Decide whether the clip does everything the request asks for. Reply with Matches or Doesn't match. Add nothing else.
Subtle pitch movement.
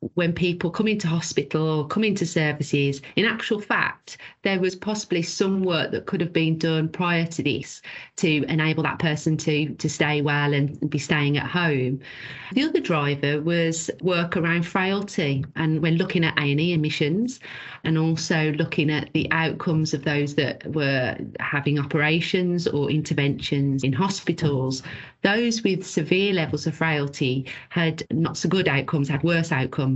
Doesn't match